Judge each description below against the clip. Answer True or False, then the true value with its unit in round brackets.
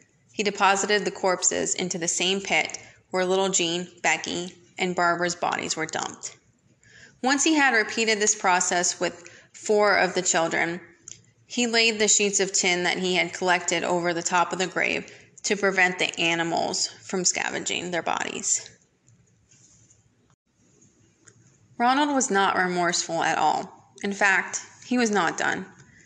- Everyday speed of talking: True (145 wpm)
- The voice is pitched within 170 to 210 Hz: True (185 Hz)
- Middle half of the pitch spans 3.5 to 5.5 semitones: False (2.9 semitones)